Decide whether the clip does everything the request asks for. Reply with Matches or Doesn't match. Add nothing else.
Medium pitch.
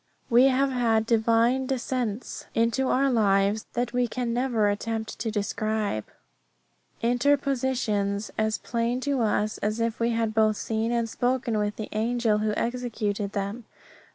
Doesn't match